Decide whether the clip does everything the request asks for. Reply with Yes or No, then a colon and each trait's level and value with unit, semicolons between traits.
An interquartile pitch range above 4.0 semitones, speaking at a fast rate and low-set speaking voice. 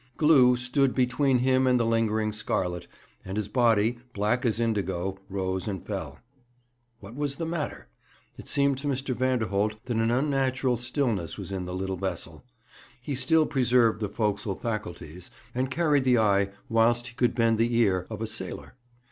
No: average, 4.4 semitones; average, 170 wpm; low, 115 Hz